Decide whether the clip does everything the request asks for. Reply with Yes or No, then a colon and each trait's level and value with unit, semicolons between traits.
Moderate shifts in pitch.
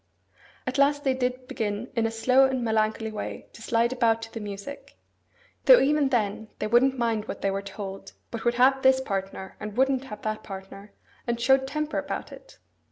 Yes: average, 3.8 semitones